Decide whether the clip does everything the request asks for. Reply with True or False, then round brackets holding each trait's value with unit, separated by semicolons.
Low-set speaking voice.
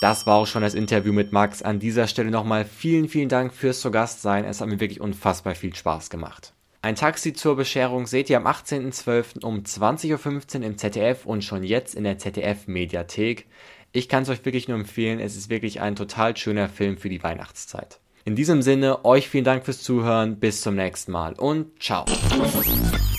True (110 Hz)